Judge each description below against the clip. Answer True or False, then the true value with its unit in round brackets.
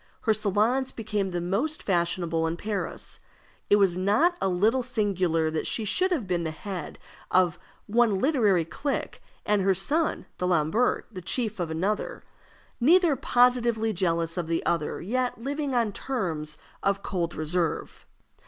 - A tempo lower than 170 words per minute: True (150 wpm)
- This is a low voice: False (200 Hz)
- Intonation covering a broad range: True (5.8 semitones)